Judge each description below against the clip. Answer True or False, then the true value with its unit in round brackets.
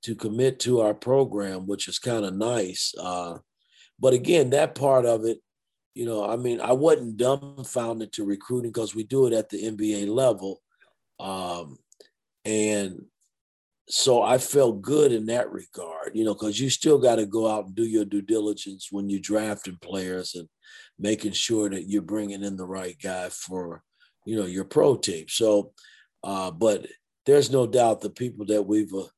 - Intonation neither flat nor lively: True (3.2 semitones)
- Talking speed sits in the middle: True (180 wpm)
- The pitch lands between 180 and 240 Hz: False (105 Hz)